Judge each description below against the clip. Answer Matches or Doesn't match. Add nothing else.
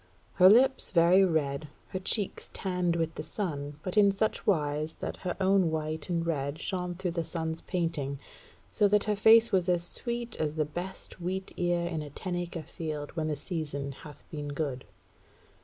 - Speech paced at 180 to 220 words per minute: Matches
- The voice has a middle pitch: Matches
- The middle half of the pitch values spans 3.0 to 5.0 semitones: Matches